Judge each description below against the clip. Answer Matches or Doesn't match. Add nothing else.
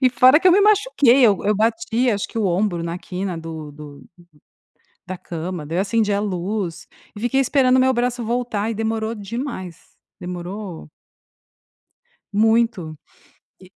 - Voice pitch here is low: Doesn't match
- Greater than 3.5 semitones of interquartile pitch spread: Matches